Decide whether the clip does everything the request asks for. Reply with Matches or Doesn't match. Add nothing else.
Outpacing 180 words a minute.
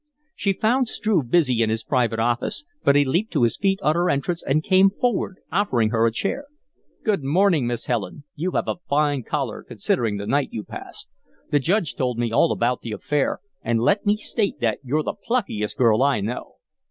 Matches